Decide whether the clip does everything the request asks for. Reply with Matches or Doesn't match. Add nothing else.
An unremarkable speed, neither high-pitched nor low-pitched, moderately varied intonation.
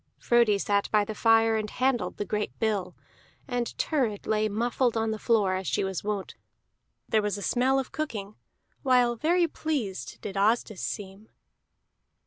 Doesn't match